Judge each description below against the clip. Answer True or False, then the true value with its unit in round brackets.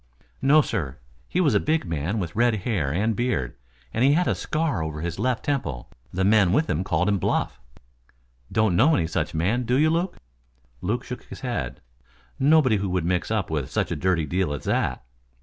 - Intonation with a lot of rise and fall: True (7.3 semitones)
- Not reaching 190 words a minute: False (200 wpm)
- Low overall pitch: True (105 Hz)